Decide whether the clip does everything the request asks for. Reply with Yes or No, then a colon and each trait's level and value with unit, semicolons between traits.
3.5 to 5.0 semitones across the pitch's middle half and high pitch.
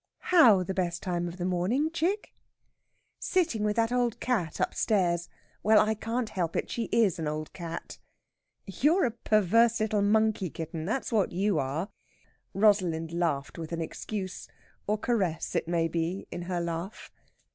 Yes: average, 4.6 semitones; high, 195 Hz